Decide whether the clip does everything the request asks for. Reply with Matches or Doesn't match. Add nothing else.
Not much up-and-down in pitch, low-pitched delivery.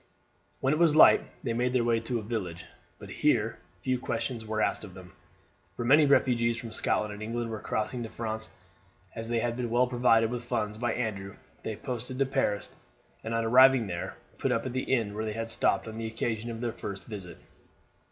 Matches